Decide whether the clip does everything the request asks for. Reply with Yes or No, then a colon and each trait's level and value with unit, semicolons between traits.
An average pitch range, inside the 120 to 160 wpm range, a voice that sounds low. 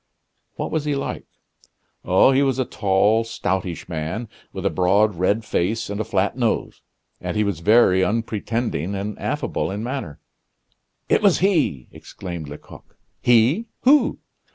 Yes: average, 4.6 semitones; average, 150 wpm; low, 105 Hz